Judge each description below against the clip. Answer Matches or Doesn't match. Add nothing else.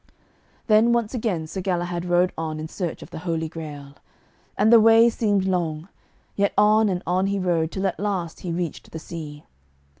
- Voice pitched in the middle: Matches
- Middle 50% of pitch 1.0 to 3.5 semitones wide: Doesn't match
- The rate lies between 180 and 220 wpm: Matches